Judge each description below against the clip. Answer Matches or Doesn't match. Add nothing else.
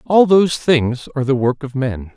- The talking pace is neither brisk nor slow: Doesn't match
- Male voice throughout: Matches